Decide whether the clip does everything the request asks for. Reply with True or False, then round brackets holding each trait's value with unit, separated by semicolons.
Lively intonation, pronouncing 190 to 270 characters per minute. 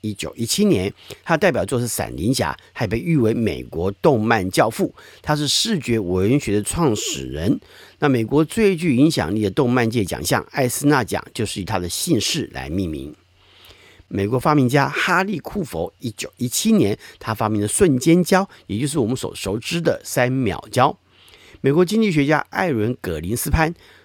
True (6.4 semitones; 265 characters per minute)